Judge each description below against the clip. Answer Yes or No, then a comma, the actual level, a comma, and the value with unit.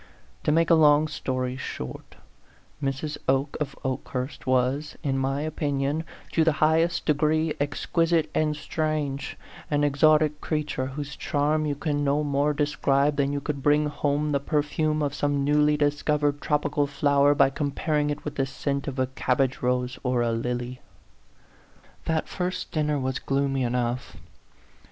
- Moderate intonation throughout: No, narrow, 1.8 semitones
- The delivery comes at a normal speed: Yes, average, 160 wpm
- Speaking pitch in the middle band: Yes, medium, 145 Hz